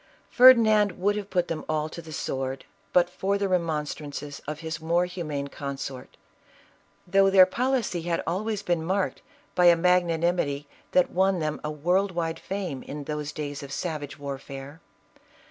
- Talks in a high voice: No, medium, 170 Hz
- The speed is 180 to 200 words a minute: No, average, 160 wpm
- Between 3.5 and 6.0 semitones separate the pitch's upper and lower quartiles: Yes, average, 4.0 semitones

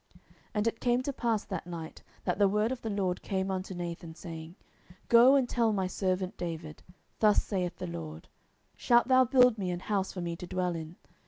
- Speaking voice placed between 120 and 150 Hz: No, high, 190 Hz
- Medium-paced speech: No, fast, 215 wpm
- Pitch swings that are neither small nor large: Yes, average, 4.6 semitones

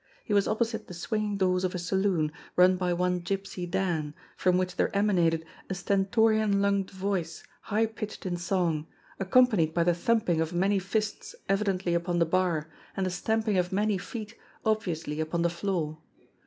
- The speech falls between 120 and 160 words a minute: No, average, 175 wpm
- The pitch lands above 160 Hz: Yes, medium, 185 Hz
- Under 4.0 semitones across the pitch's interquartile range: Yes, average, 2.8 semitones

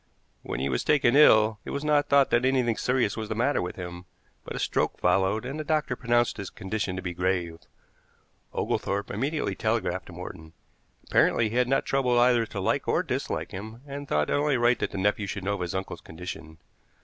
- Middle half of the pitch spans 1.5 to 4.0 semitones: No, average, 5.3 semitones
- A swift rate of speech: Yes, fast, 210 wpm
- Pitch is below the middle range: Yes, low, 110 Hz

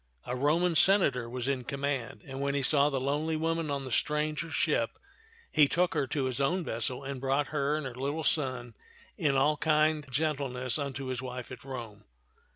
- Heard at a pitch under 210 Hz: Yes, medium, 140 Hz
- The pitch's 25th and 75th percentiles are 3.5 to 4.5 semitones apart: No, average, 2.8 semitones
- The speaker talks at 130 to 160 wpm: No, average, 190 wpm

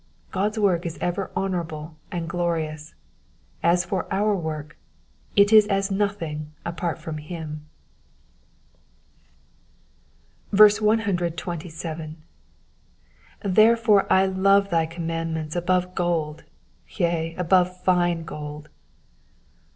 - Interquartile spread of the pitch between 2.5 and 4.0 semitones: Yes, average, 3.2 semitones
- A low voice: No, medium, 175 Hz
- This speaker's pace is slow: Yes, slow, 95 wpm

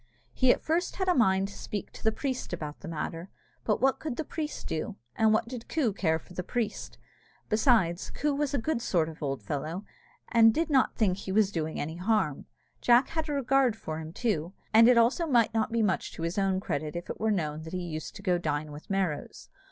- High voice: Yes, high, 205 Hz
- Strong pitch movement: Yes, wide, 6.7 semitones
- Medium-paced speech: No, fast, 235 wpm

